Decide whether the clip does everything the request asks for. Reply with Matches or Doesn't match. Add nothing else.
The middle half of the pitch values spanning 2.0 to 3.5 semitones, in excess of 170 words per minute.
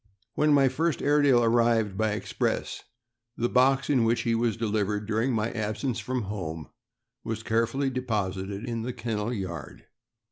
Doesn't match